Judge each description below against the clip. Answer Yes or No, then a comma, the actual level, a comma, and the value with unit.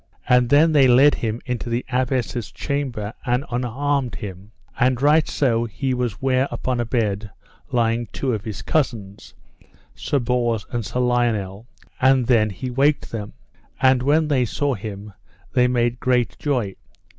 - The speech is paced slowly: No, average, 155 wpm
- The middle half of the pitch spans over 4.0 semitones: No, average, 2.7 semitones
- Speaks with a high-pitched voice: No, low, 125 Hz